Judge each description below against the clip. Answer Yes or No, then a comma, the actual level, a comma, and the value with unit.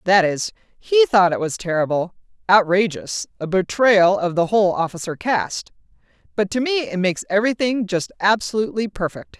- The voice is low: No, high, 200 Hz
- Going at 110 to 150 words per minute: Yes, slow, 135 wpm